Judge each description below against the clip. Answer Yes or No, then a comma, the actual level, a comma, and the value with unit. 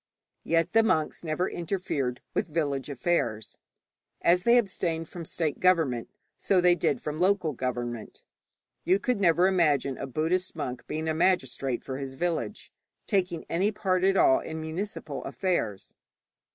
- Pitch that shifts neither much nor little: Yes, average, 4.9 semitones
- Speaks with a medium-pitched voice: Yes, medium, 165 Hz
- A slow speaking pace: No, average, 150 wpm